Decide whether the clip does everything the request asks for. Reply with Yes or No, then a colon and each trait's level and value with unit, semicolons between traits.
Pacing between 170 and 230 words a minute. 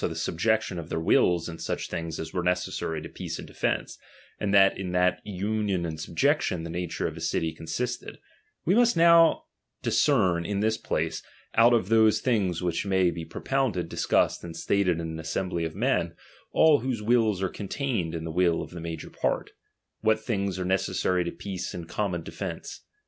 Yes: average, 190 wpm